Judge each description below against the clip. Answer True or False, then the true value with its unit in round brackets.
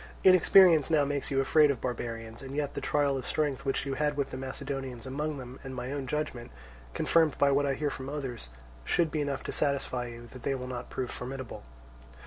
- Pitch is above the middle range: False (135 Hz)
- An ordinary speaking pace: False (215 wpm)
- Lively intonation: False (2.4 semitones)